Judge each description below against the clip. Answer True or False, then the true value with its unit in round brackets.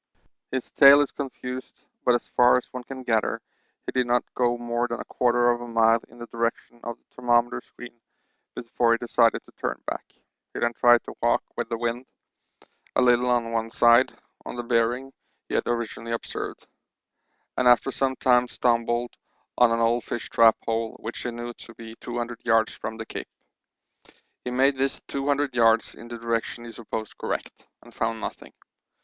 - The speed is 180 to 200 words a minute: True (185 wpm)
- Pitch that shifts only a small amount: True (1.1 semitones)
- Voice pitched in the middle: False (120 Hz)